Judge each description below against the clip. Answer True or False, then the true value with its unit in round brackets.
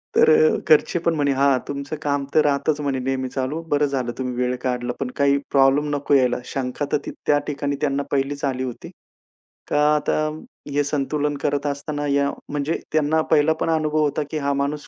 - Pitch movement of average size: False (1.5 semitones)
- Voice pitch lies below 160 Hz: True (140 Hz)